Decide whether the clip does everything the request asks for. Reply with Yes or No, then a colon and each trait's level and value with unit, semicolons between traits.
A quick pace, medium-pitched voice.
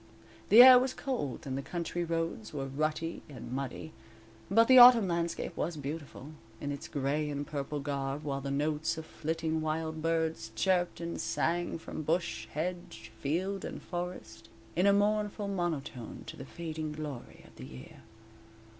No: average, 165 wpm; medium, 160 Hz